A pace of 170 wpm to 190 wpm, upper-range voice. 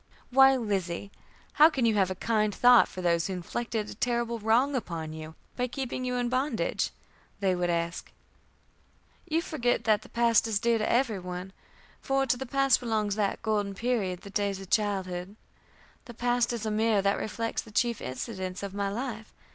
Yes: average, 185 wpm; high, 220 Hz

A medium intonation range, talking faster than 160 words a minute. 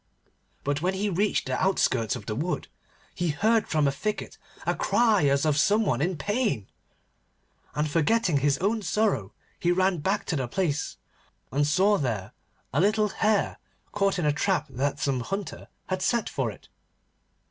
No: wide, 6.1 semitones; average, 175 wpm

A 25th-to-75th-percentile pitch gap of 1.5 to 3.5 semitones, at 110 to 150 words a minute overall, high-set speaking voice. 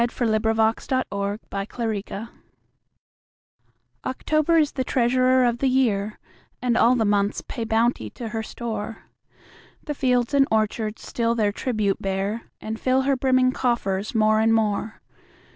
Yes: average, 3.0 semitones; average, 140 wpm; high, 230 Hz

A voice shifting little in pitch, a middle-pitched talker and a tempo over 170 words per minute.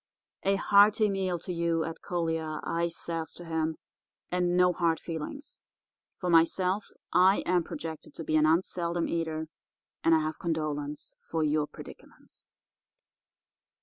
No: narrow, 2.1 semitones; medium, 165 Hz; average, 140 wpm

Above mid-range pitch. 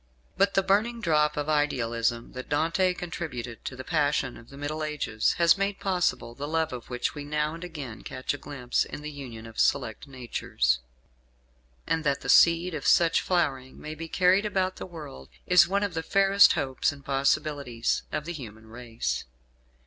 No: medium, 150 Hz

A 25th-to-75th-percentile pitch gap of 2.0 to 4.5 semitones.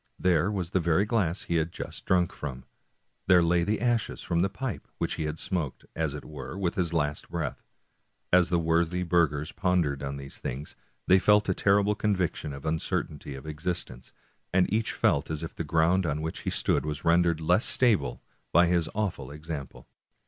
Yes: average, 3.4 semitones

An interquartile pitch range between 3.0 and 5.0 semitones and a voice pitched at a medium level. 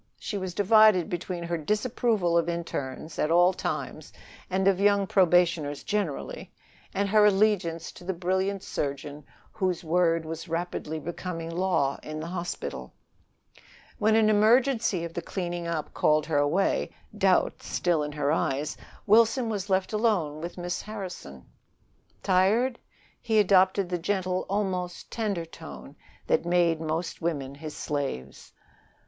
Yes: average, 3.7 semitones; medium, 175 Hz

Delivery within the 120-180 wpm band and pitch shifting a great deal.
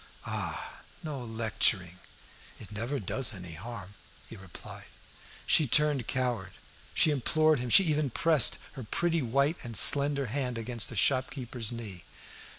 No: average, 140 wpm; average, 4.4 semitones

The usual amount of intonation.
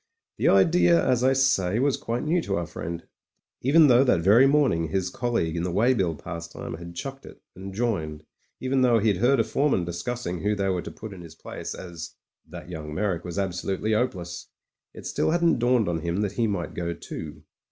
No: wide, 6.1 semitones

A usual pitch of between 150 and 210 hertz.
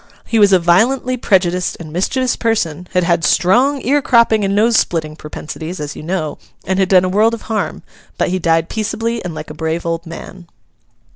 Yes: medium, 185 Hz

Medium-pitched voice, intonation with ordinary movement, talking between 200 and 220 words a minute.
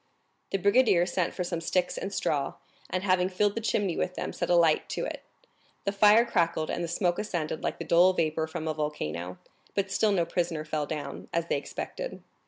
Yes: medium, 175 Hz; average, 3.6 semitones; fast, 205 wpm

